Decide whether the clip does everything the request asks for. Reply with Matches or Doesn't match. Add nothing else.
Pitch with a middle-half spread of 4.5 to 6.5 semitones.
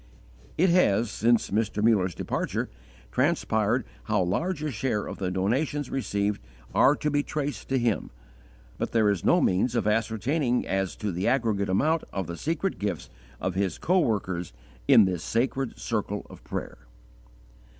Matches